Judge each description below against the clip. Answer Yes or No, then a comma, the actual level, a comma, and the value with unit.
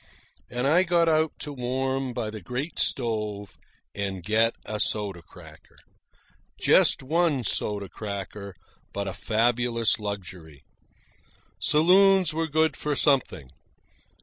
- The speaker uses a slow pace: Yes, slow, 120 wpm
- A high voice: No, low, 120 Hz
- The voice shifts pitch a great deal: Yes, wide, 6.7 semitones